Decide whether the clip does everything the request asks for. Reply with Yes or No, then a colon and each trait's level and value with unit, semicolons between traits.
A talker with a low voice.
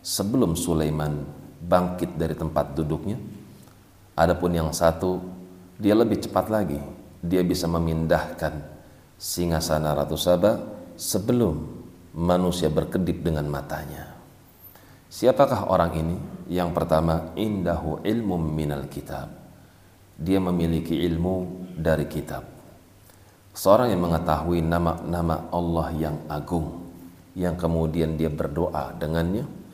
Yes: very low, 85 Hz